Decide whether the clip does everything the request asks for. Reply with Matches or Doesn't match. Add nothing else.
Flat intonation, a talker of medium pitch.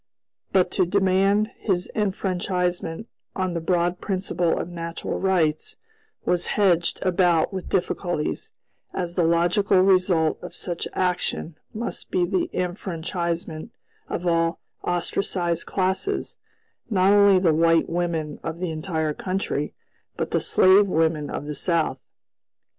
Matches